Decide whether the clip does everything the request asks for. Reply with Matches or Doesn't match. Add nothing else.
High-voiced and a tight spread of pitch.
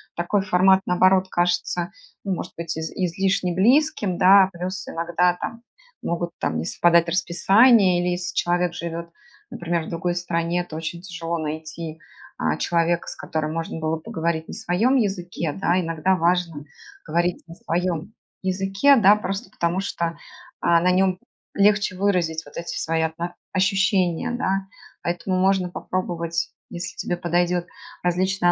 Doesn't match